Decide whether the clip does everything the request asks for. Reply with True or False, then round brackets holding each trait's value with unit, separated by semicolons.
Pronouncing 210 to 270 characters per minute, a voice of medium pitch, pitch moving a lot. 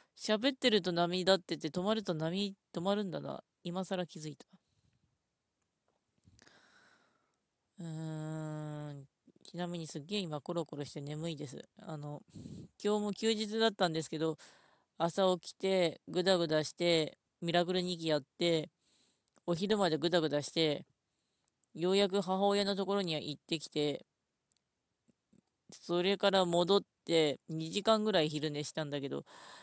False (260 characters per minute; 175 Hz; 3.9 semitones)